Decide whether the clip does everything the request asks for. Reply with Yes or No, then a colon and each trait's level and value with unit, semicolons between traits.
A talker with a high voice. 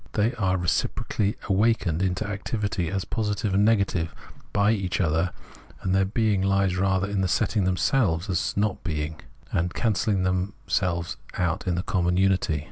No: very low, 95 Hz